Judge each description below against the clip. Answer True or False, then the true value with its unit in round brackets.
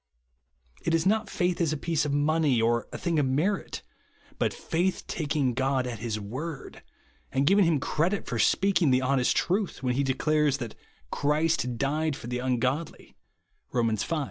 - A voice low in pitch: False (145 Hz)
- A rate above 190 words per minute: False (185 wpm)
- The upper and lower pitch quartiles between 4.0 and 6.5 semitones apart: True (4.5 semitones)